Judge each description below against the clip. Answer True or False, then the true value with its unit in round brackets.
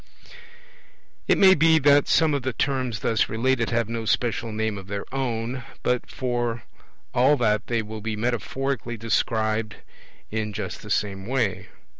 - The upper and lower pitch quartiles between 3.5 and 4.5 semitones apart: False (3.1 semitones)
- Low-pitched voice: True (115 Hz)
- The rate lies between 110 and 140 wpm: False (155 wpm)